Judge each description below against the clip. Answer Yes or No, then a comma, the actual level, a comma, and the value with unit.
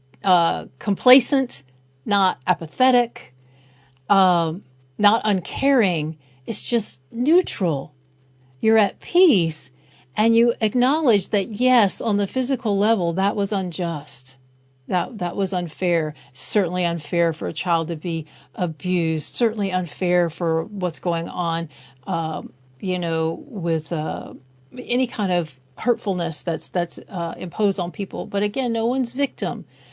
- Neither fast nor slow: No, slow, 130 wpm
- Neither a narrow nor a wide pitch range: Yes, average, 4.9 semitones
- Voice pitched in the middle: Yes, medium, 180 Hz